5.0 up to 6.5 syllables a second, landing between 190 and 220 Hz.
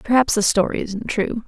Yes: 5.1 syllables/s; high, 215 Hz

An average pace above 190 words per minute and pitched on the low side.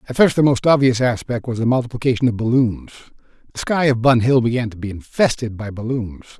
Yes: fast, 205 wpm; low, 120 Hz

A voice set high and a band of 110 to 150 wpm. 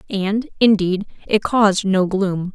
Yes: high, 200 Hz; average, 140 wpm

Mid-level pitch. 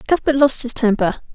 No: very high, 255 Hz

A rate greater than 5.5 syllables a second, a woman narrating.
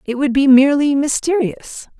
No: 5.0 syllables/s; female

